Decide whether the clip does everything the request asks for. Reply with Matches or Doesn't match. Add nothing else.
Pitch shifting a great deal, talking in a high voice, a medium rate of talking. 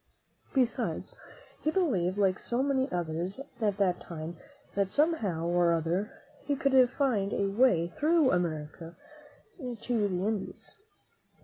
Doesn't match